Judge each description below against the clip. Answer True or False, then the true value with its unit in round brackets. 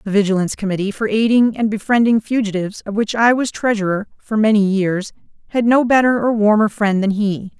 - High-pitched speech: True (215 Hz)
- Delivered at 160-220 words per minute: True (190 wpm)